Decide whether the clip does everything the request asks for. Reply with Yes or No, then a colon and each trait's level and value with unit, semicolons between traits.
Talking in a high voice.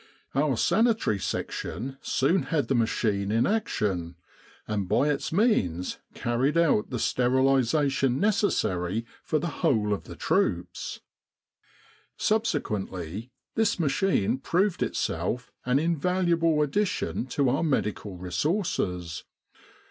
No: low, 135 Hz